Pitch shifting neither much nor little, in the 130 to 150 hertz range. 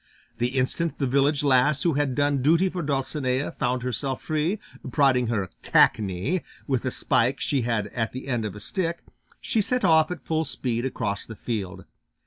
Yes: average, 4.3 semitones; low, 135 Hz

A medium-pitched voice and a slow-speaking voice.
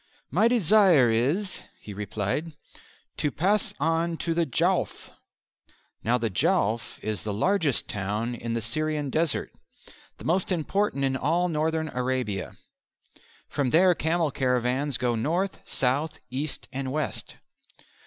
Yes: medium, 145 Hz; slow, 130 wpm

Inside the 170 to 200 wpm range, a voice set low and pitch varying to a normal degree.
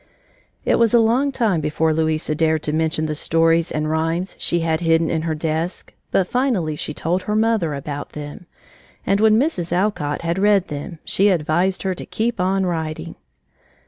No: average, 180 wpm; medium, 165 Hz; average, 3.8 semitones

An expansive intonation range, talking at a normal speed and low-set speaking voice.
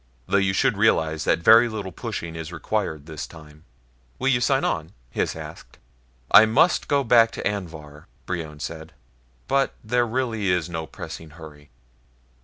Yes: wide, 6.2 semitones; average, 160 wpm; very low, 90 Hz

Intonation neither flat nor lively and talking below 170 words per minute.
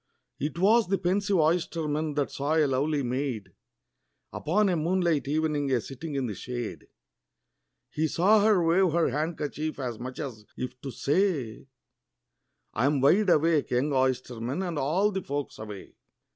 Yes: average, 4.7 semitones; average, 155 wpm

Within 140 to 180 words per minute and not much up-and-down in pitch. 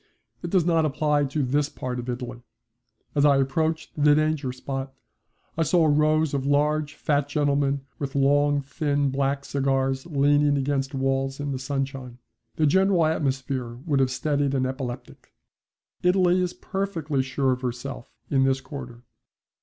Yes: average, 155 wpm; narrow, 2.2 semitones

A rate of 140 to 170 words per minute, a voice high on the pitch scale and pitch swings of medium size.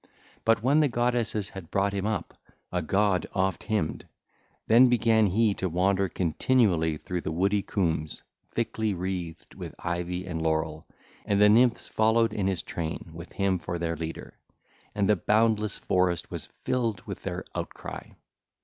No: average, 160 wpm; very low, 95 Hz; average, 4.2 semitones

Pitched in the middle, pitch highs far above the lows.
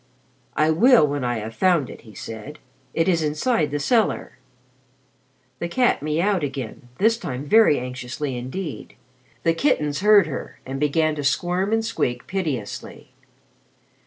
Yes: medium, 150 Hz; wide, 6.0 semitones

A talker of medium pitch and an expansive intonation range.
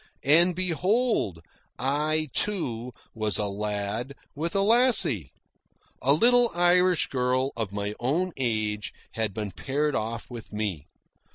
No: low, 130 Hz; wide, 8.5 semitones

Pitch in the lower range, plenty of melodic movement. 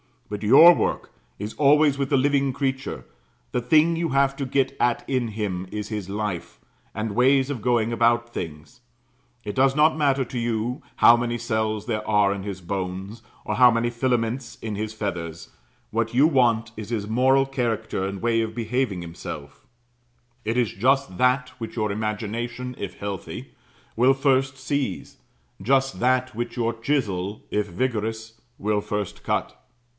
No: low, 115 Hz; average, 3.9 semitones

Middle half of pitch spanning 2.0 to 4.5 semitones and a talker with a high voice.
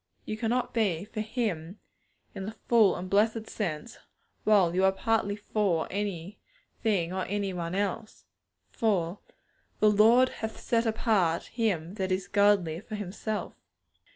Yes: average, 3.1 semitones; high, 205 Hz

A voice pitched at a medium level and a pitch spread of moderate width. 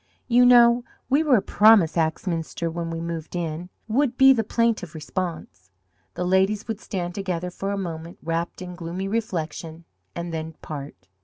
Yes: medium, 180 Hz; average, 4.6 semitones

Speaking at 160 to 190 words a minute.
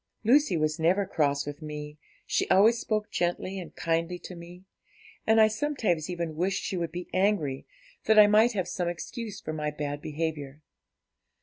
Yes: average, 175 wpm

